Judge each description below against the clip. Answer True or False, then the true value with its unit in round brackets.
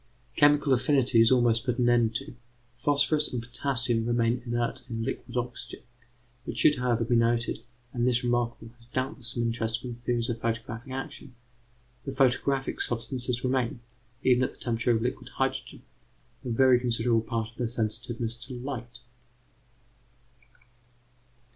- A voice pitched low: True (120 Hz)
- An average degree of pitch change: False (1.6 semitones)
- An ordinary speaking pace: True (150 wpm)